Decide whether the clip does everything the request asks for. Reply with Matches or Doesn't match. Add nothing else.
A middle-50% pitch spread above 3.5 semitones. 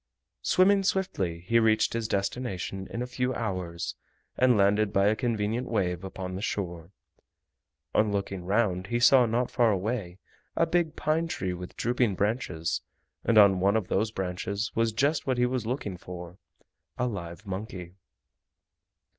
Matches